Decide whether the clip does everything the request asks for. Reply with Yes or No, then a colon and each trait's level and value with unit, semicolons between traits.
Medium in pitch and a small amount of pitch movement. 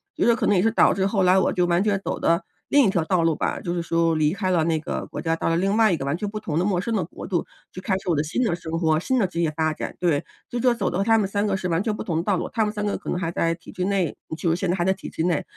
No: medium, 180 Hz; average, 3.5 semitones